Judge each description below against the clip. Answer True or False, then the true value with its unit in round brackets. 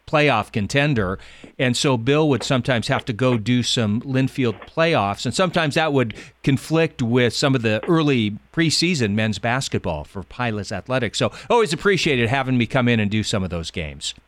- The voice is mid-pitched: False (125 Hz)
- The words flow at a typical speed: True (180 wpm)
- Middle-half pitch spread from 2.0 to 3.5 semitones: False (5.0 semitones)